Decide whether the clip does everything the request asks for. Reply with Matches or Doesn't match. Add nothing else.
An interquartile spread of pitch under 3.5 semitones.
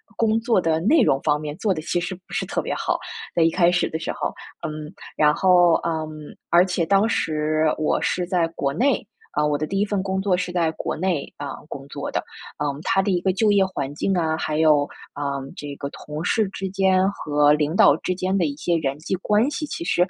Doesn't match